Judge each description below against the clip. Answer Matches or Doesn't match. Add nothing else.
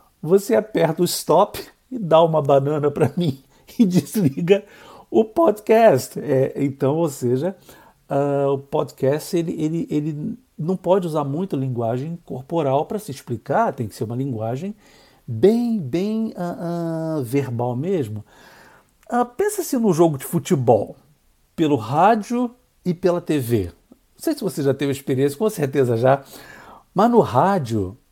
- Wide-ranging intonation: Matches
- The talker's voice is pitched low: Doesn't match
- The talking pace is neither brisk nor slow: Matches